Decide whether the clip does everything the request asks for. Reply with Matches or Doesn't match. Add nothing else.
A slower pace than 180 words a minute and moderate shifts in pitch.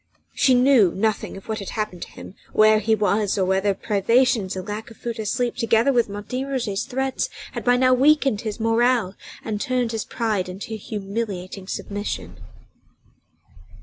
Matches